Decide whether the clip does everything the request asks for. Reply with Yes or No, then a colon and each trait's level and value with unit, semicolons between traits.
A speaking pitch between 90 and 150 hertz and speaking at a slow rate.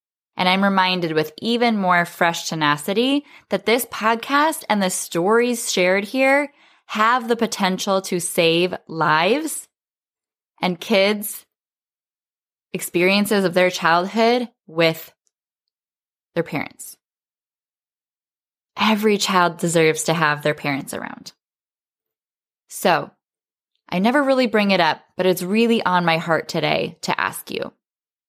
No: high, 190 Hz; slow, 120 wpm